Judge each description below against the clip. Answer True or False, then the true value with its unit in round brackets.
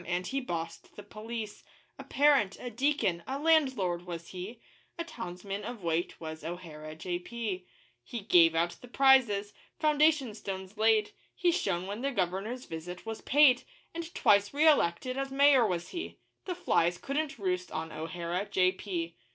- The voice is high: True (205 Hz)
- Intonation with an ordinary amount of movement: False (7.1 semitones)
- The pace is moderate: True (160 wpm)